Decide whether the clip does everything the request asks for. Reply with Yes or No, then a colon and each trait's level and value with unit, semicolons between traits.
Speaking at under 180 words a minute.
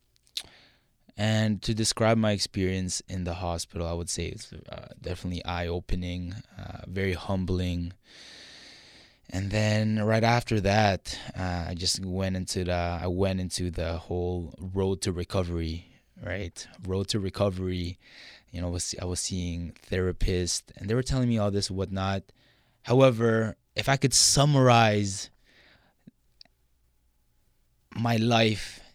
Yes: slow, 135 wpm